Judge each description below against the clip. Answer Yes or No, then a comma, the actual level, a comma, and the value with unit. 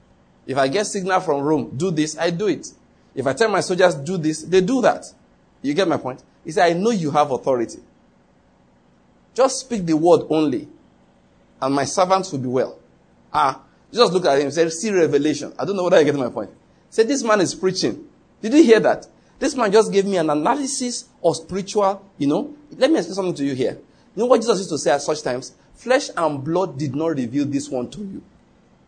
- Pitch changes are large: Yes, wide, 7.0 semitones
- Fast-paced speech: Yes, fast, 220 wpm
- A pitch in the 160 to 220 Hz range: Yes, medium, 170 Hz